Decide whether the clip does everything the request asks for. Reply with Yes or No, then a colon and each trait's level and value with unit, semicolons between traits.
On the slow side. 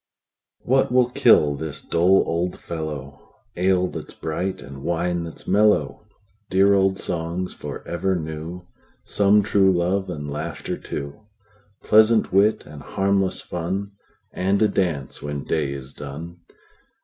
Yes: slow, 125 wpm